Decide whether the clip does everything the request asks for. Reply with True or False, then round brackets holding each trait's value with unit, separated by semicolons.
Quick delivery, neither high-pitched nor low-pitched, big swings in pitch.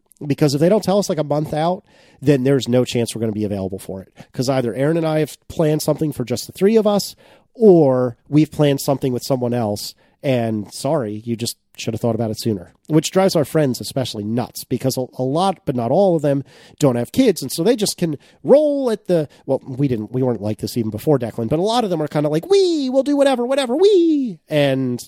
True (245 wpm; 145 Hz; 6.3 semitones)